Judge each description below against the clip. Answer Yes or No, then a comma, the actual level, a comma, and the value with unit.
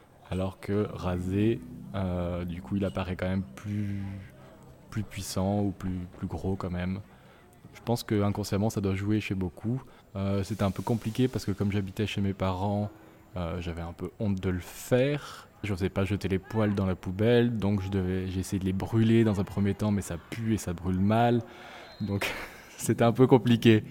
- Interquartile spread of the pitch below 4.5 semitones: Yes, narrow, 2.4 semitones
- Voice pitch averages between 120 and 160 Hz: No, low, 100 Hz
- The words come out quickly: No, average, 200 wpm